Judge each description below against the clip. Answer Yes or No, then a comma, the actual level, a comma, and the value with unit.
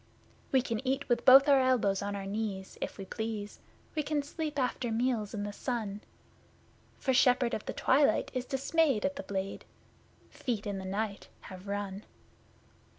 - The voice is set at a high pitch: Yes, high, 230 Hz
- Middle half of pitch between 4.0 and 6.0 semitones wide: Yes, average, 4.7 semitones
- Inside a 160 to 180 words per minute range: Yes, average, 170 wpm